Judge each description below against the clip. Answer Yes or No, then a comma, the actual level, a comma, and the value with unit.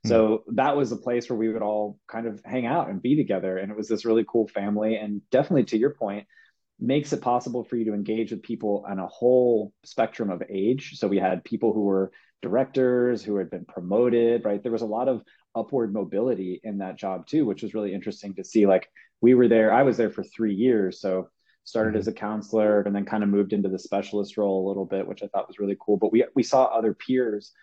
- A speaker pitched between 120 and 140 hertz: No, low, 110 Hz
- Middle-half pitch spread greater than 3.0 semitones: No, narrow, 2.4 semitones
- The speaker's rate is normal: No, fast, 240 wpm